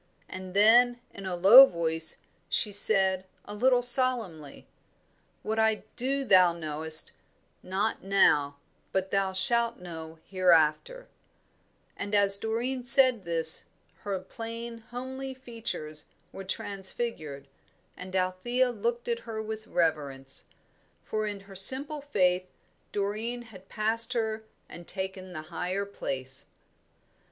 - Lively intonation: No, average, 4.5 semitones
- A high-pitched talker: Yes, high, 200 Hz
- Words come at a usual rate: No, slow, 120 wpm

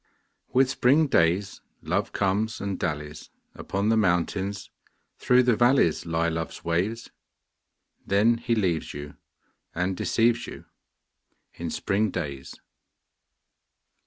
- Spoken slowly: Yes, slow, 110 wpm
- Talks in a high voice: No, low, 100 Hz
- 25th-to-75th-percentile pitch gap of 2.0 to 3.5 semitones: No, wide, 5.5 semitones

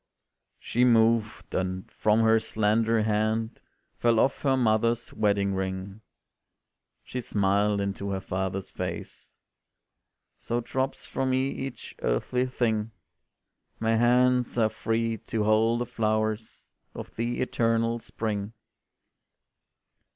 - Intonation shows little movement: Yes, narrow, 2.1 semitones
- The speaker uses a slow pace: Yes, slow, 115 wpm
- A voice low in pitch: Yes, low, 110 Hz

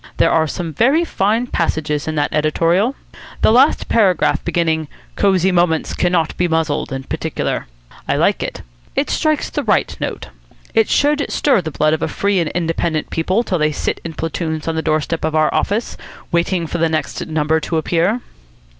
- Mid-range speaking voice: Yes, medium, 165 Hz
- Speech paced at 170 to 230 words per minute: Yes, average, 180 wpm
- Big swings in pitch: No, average, 3.9 semitones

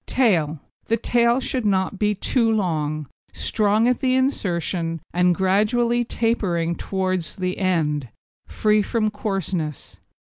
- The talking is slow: Yes, slow, 125 wpm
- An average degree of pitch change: Yes, average, 4.9 semitones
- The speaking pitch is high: Yes, high, 195 Hz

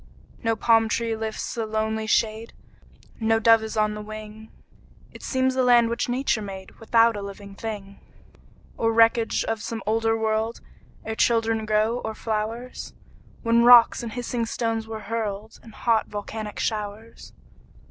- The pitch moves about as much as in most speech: No, narrow, 1.1 semitones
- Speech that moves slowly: No, average, 155 wpm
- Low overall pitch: No, high, 225 Hz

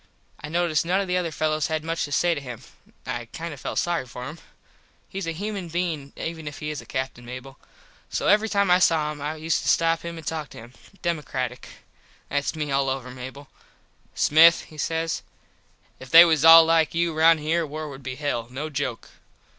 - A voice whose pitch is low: No, medium, 155 Hz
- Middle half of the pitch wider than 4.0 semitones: No, average, 3.1 semitones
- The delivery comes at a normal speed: No, fast, 210 wpm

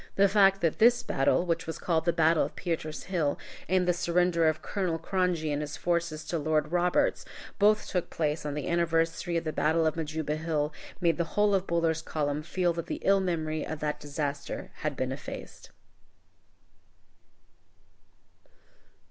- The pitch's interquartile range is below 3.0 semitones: Yes, narrow, 2.4 semitones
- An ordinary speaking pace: Yes, average, 170 wpm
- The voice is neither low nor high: Yes, medium, 165 Hz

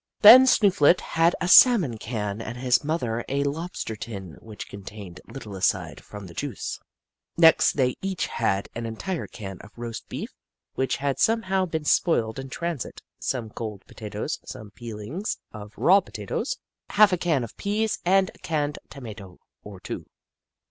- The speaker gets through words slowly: No, average, 160 wpm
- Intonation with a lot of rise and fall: Yes, wide, 8.2 semitones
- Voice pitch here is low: Yes, low, 130 Hz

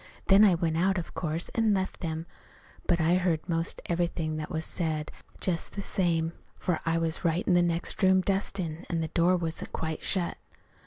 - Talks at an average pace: Yes, average, 195 wpm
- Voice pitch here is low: No, medium, 170 Hz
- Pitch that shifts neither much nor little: No, narrow, 2.2 semitones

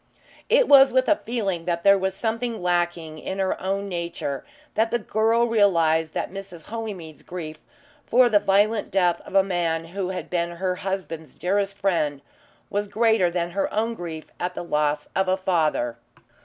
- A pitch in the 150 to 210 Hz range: Yes, high, 190 Hz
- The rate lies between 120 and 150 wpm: No, average, 175 wpm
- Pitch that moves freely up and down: No, average, 3.4 semitones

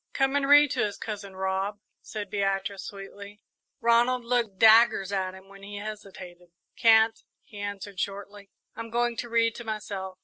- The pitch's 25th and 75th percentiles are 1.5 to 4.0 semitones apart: Yes, average, 2.7 semitones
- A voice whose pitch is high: Yes, high, 205 Hz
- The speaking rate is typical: Yes, average, 165 wpm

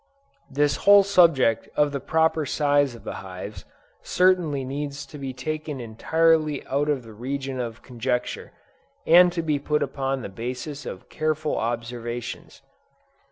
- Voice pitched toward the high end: No, medium, 140 Hz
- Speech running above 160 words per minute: No, average, 140 wpm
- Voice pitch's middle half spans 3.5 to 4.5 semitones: Yes, average, 4.0 semitones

